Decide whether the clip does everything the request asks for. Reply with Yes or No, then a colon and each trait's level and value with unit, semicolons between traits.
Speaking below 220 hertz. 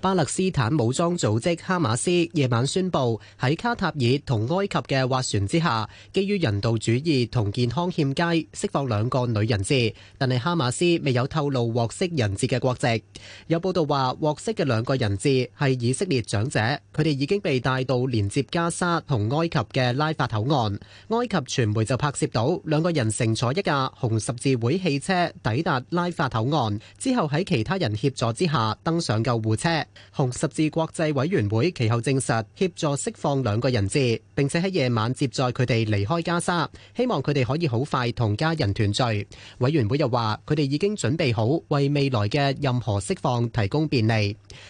Yes: low, 135 Hz